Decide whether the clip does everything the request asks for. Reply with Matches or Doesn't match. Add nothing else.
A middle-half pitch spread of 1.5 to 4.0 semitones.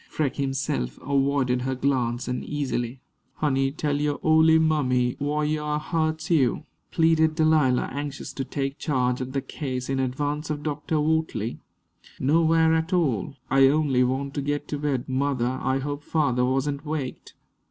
Matches